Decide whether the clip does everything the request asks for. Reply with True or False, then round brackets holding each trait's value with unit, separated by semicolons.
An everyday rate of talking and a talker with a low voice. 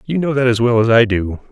False (320 wpm; 120 Hz)